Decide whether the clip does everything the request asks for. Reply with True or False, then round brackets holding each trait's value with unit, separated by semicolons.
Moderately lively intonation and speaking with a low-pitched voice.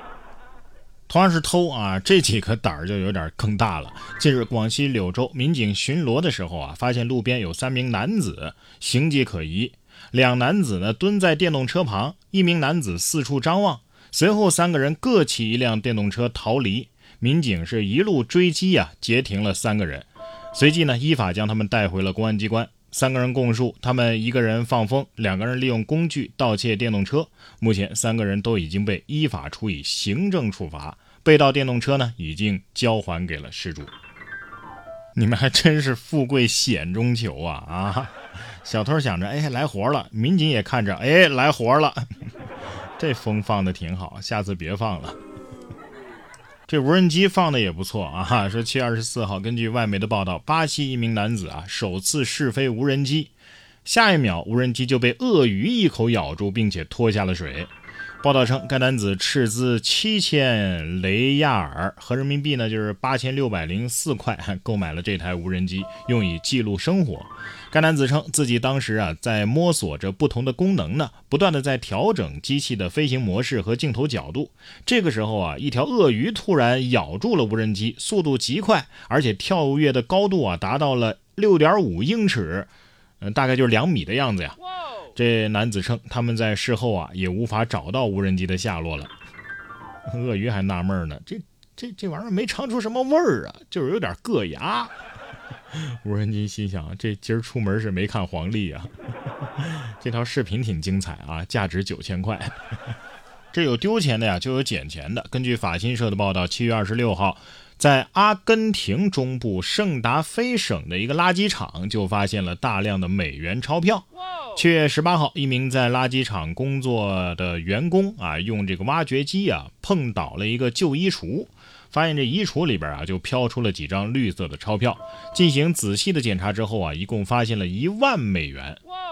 False (6.3 semitones; 120 Hz)